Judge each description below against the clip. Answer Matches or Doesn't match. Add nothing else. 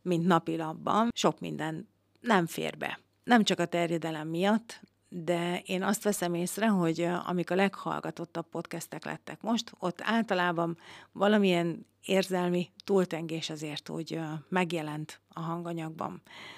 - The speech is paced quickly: Doesn't match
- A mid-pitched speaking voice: Matches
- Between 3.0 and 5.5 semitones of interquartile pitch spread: Doesn't match